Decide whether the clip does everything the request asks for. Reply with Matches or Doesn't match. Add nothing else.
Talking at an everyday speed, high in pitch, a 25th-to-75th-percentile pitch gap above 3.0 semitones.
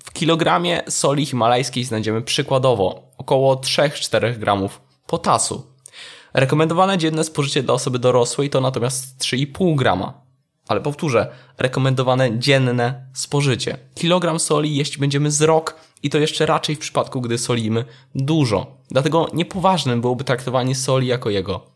Doesn't match